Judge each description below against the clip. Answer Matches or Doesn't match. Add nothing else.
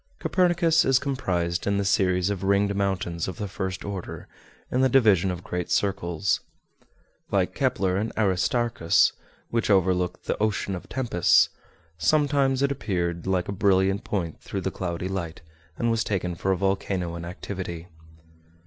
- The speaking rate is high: Doesn't match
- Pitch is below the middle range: Matches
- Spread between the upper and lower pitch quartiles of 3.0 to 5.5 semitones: Matches